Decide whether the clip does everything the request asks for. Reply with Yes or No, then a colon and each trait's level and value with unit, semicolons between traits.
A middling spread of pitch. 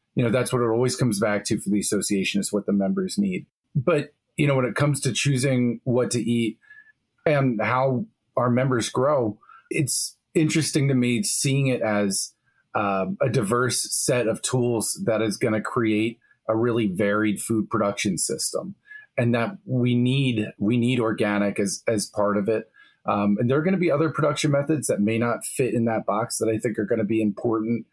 Yes: average, 4.0 semitones